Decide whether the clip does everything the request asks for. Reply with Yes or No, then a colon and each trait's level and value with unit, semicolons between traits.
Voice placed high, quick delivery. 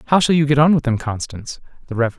No: low, 135 Hz; fast, 275 wpm